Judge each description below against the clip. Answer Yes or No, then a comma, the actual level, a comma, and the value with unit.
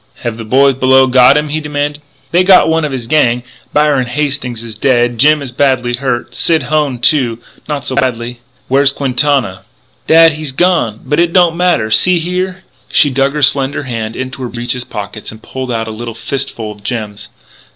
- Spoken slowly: No, average, 195 wpm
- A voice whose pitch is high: No, low, 130 Hz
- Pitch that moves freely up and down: No, average, 3.8 semitones